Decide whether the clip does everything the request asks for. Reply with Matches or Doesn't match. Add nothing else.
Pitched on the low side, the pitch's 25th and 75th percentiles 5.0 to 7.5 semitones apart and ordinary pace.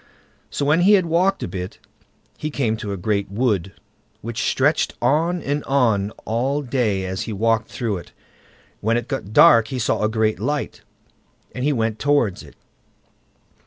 Matches